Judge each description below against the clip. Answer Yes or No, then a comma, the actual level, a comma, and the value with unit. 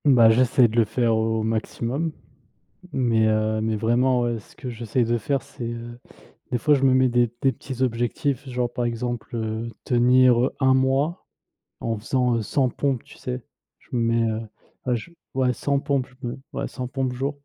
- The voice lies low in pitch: Yes, low, 120 Hz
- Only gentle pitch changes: Yes, narrow, 2.3 semitones